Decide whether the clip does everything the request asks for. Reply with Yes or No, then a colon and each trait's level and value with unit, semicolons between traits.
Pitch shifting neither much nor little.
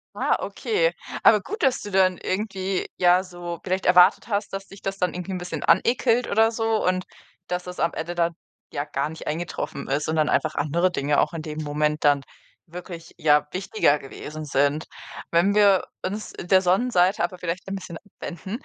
Yes: average, 3.5 semitones